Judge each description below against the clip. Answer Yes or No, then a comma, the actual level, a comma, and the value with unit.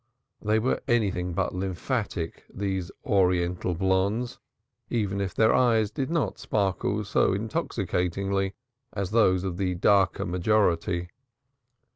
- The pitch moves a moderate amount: Yes, average, 3.0 semitones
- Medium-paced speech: No, slow, 110 wpm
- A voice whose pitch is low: Yes, very low, 95 Hz